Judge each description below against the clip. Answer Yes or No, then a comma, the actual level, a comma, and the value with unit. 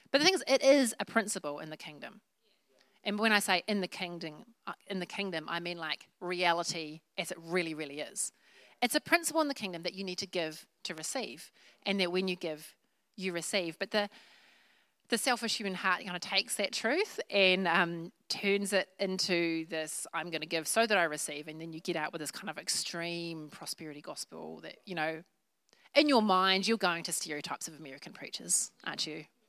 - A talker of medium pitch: Yes, medium, 180 Hz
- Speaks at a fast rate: Yes, fast, 210 wpm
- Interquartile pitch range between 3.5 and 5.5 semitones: Yes, average, 4.1 semitones